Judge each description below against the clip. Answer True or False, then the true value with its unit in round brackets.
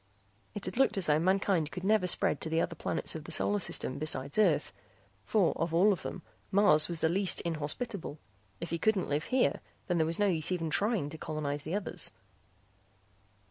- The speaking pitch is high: False (170 Hz)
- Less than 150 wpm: False (195 wpm)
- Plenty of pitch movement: False (4.3 semitones)